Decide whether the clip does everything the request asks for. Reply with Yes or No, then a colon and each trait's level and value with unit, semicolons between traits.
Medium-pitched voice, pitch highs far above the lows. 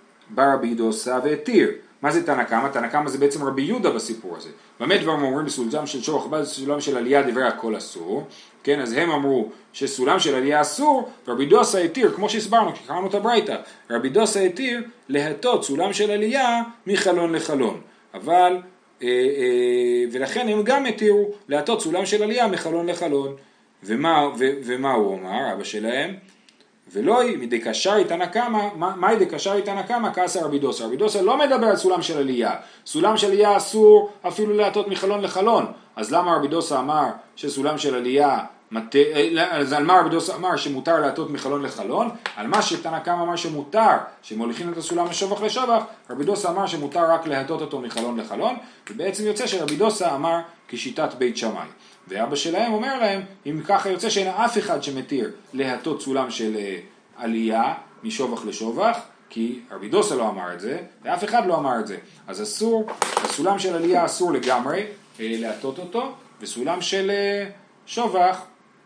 Yes: medium, 180 Hz; wide, 6.8 semitones